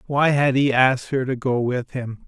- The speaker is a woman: No, male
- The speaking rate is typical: No, fast, 235 wpm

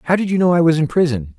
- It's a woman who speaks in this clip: No, male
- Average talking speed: No, fast, 345 wpm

